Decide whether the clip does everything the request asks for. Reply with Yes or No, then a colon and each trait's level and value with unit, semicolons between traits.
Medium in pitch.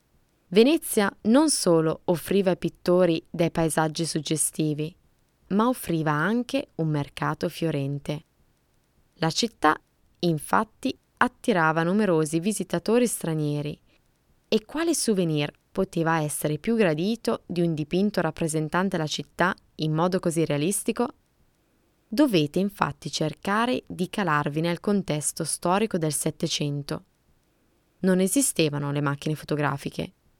Yes: medium, 170 Hz